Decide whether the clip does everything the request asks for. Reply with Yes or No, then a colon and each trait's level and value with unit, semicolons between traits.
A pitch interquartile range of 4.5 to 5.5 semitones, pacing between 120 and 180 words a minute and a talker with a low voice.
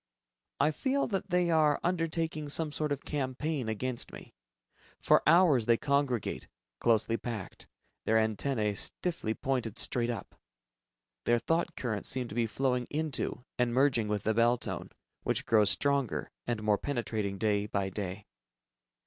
Yes: average, 5.2 semitones; average, 150 wpm; low, 125 Hz